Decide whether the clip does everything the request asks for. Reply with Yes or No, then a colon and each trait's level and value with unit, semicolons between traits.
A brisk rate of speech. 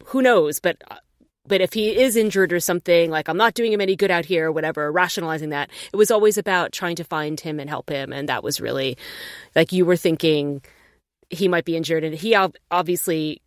Yes: fast, 225 wpm